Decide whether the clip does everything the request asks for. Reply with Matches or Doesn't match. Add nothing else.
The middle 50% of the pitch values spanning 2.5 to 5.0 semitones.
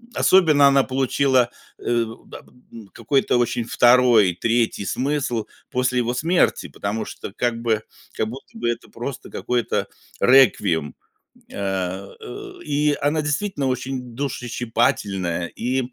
Matches